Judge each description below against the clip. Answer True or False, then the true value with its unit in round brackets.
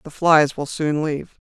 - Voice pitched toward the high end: False (150 Hz)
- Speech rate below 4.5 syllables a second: False (4.7 syllables/s)